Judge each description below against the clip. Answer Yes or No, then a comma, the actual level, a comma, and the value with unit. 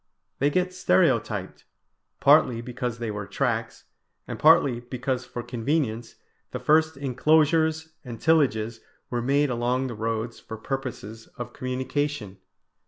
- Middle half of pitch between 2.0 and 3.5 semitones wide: No, average, 4.1 semitones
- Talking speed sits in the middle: No, slow, 125 wpm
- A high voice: No, low, 125 Hz